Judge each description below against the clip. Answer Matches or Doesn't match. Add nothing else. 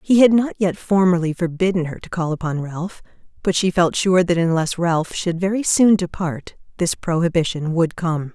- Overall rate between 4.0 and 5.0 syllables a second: Matches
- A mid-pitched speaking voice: Matches